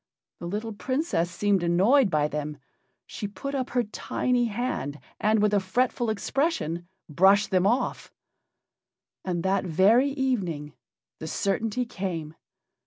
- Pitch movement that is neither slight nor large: No, wide, 5.9 semitones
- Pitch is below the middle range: No, high, 200 Hz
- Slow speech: Yes, slow, 130 wpm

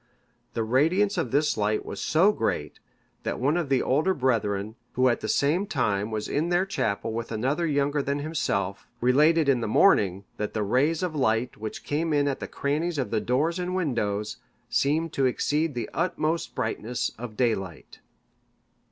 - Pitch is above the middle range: No, low, 135 Hz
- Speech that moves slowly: No, average, 180 wpm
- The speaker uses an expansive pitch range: Yes, wide, 6.2 semitones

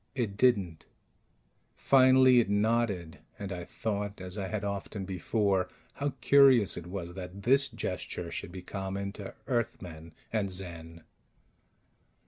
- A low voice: Yes, low, 100 Hz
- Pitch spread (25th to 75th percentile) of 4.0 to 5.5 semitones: Yes, average, 4.4 semitones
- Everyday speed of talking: No, slow, 130 wpm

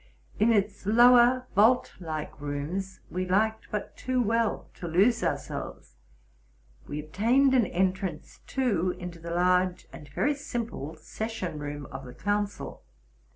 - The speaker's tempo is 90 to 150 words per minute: Yes, slow, 135 wpm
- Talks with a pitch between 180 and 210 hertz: Yes, high, 190 Hz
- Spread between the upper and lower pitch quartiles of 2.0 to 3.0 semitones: No, wide, 5.6 semitones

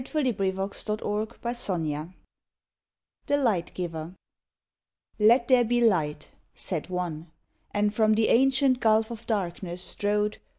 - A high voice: Yes, high, 210 Hz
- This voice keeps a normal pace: No, slow, 115 wpm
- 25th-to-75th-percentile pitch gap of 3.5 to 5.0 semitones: Yes, average, 4.7 semitones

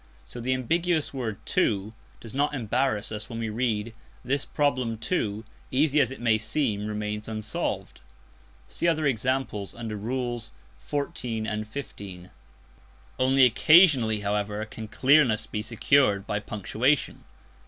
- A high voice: No, low, 115 Hz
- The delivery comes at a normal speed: No, slow, 130 wpm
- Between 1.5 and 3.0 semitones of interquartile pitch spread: No, average, 3.9 semitones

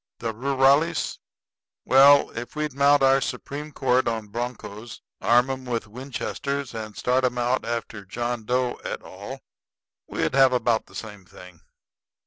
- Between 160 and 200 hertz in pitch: No, low, 125 Hz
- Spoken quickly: No, average, 145 wpm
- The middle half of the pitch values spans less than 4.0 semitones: Yes, average, 2.9 semitones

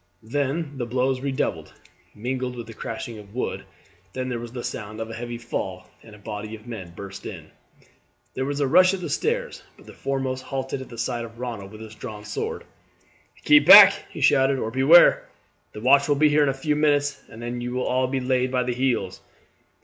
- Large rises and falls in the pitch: No, average, 3.4 semitones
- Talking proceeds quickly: Yes, fast, 215 wpm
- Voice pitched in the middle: No, low, 125 Hz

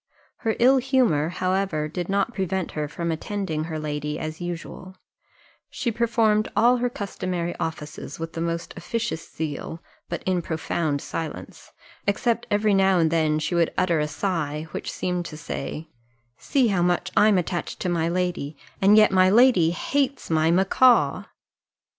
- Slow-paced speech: No, average, 160 wpm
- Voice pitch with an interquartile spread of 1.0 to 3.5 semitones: No, average, 4.4 semitones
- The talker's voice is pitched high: No, medium, 175 Hz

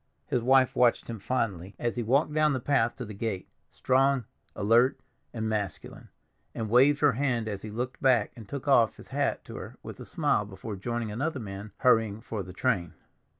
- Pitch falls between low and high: No, low, 115 Hz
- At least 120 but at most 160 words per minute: No, average, 195 wpm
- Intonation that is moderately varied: Yes, average, 3.7 semitones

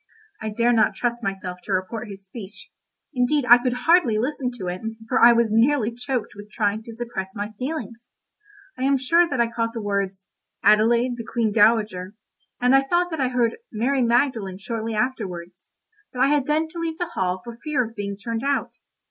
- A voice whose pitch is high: Yes, high, 235 Hz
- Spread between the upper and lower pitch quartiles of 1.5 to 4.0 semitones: Yes, average, 3.7 semitones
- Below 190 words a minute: No, average, 195 wpm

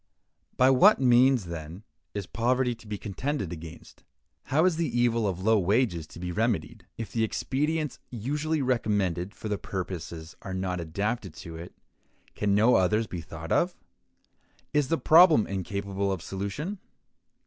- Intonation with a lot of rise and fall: Yes, wide, 5.7 semitones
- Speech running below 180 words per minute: Yes, average, 155 wpm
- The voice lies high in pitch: No, low, 105 Hz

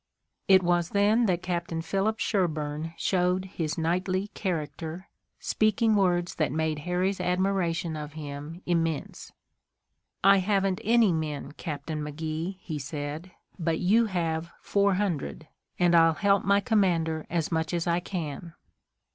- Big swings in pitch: No, average, 3.3 semitones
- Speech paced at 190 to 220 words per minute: No, slow, 135 wpm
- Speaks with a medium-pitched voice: Yes, medium, 175 Hz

